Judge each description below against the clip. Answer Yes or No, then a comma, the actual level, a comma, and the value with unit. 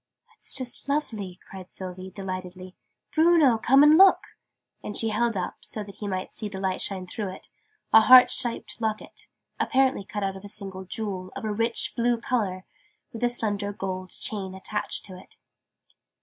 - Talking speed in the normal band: Yes, average, 175 wpm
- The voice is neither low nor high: No, high, 205 Hz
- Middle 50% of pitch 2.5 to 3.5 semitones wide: No, average, 4.0 semitones